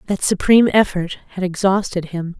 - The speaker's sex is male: No, female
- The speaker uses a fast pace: No, average, 150 wpm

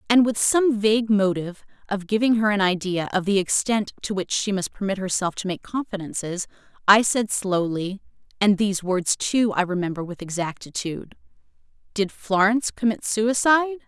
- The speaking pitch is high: Yes, high, 200 Hz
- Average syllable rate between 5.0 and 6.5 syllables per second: Yes, 5.3 syllables/s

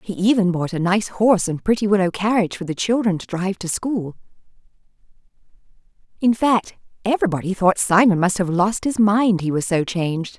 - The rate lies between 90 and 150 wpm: No, average, 180 wpm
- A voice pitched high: Yes, high, 195 Hz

